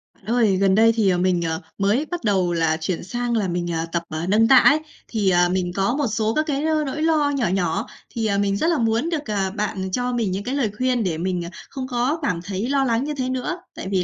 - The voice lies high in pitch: Yes, high, 215 Hz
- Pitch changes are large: Yes, wide, 5.7 semitones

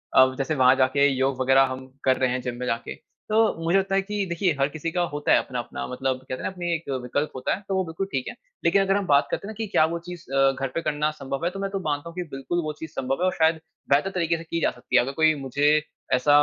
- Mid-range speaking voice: Yes, medium, 150 Hz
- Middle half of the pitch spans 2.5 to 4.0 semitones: No, average, 4.6 semitones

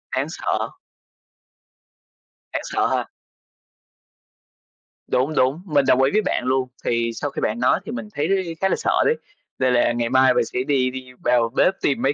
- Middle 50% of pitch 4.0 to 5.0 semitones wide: No, average, 2.8 semitones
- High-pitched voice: No, low, 130 Hz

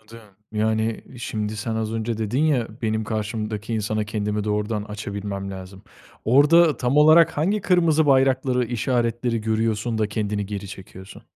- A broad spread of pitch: No, average, 3.0 semitones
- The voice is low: Yes, low, 110 Hz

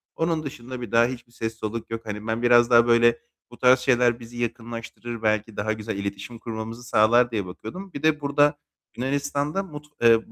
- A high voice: No, low, 120 Hz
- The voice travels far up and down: No, narrow, 2.4 semitones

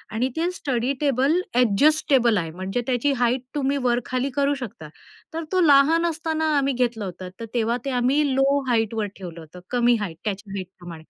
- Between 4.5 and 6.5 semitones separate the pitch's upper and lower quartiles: Yes, average, 5.1 semitones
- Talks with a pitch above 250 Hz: No, high, 245 Hz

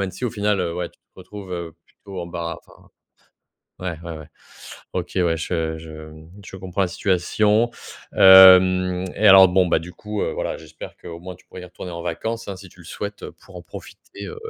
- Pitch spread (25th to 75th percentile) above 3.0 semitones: No, narrow, 2.4 semitones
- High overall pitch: No, very low, 90 Hz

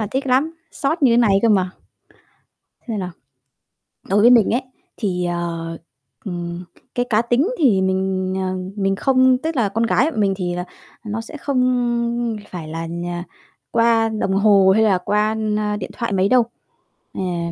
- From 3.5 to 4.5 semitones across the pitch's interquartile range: Yes, average, 4.2 semitones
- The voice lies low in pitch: No, high, 210 Hz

